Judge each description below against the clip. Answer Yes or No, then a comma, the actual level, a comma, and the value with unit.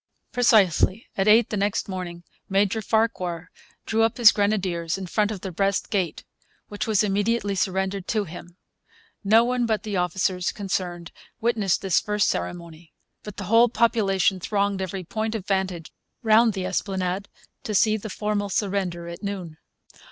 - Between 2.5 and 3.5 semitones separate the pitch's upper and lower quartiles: Yes, average, 2.8 semitones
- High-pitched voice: Yes, high, 200 Hz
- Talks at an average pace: Yes, average, 160 wpm